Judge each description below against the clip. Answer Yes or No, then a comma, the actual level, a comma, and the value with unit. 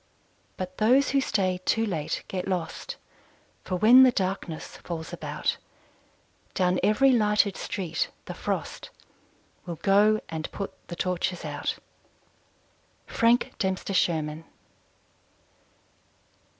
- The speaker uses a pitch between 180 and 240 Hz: Yes, high, 190 Hz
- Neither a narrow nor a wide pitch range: Yes, average, 3.5 semitones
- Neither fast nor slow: No, slow, 110 wpm